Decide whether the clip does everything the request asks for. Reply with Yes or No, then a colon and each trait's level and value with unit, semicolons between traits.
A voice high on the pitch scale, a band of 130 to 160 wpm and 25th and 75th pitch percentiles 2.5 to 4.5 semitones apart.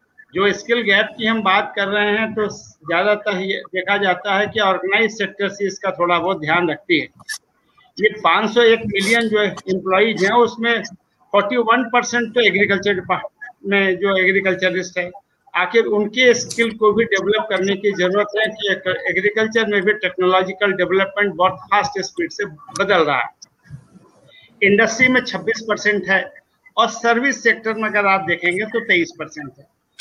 Yes: high, 205 Hz; average, 155 wpm; average, 2.9 semitones